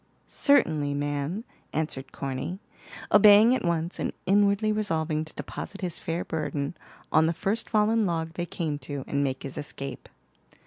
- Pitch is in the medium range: Yes, medium, 165 Hz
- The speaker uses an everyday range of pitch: No, wide, 5.8 semitones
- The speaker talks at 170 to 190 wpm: No, average, 150 wpm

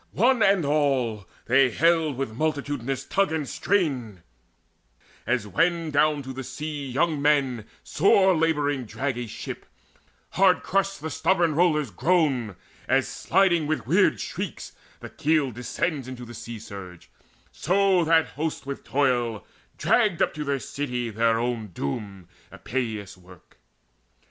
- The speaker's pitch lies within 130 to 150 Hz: Yes, medium, 140 Hz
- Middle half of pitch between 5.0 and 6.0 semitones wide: Yes, average, 5.3 semitones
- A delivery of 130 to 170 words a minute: Yes, average, 140 wpm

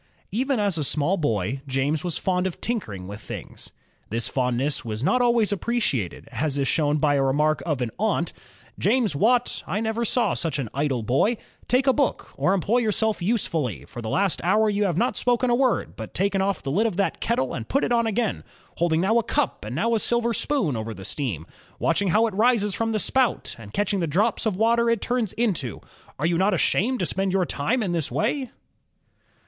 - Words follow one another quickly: Yes, fast, 215 wpm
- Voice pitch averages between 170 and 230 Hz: Yes, high, 190 Hz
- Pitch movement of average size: No, wide, 8.2 semitones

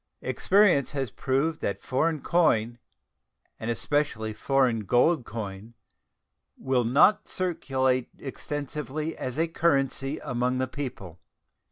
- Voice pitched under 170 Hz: Yes, low, 135 Hz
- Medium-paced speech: No, slow, 110 wpm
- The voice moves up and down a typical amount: Yes, average, 4.1 semitones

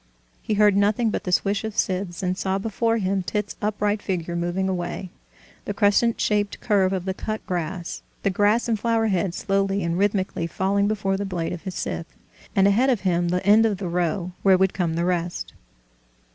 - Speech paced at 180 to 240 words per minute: Yes, average, 200 wpm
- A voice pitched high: Yes, high, 195 Hz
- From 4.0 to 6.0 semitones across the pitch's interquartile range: No, narrow, 2.4 semitones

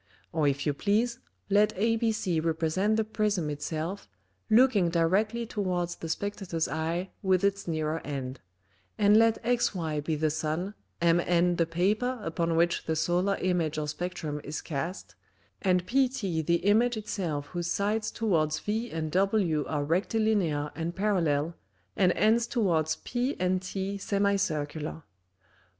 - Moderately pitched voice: Yes, medium, 180 Hz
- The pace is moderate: Yes, average, 145 wpm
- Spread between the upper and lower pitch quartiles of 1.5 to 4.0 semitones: No, average, 4.7 semitones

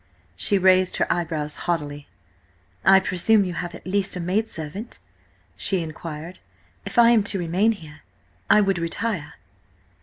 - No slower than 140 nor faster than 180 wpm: Yes, average, 145 wpm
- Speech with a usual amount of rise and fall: Yes, average, 3.4 semitones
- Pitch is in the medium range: Yes, medium, 180 Hz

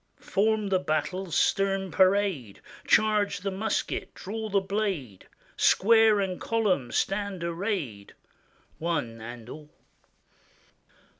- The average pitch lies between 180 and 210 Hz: Yes, high, 190 Hz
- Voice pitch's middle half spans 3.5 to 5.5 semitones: Yes, average, 4.7 semitones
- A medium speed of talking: No, slow, 100 wpm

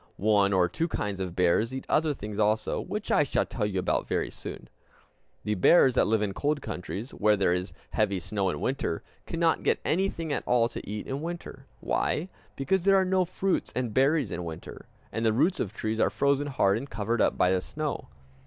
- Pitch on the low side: Yes, low, 115 Hz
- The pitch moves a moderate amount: No, wide, 7.0 semitones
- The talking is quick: Yes, fast, 210 wpm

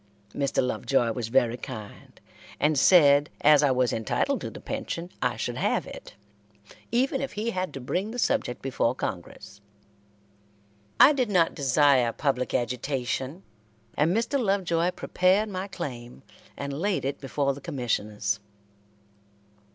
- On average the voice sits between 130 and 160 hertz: Yes, medium, 140 Hz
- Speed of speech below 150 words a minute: Yes, average, 140 wpm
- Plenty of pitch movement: Yes, wide, 6.6 semitones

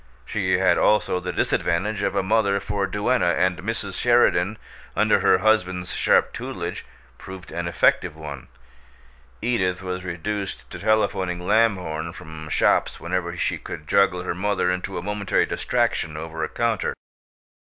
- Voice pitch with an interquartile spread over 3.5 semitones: No, average, 3.0 semitones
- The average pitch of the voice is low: Yes, very low, 90 Hz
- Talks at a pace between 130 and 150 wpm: Yes, average, 145 wpm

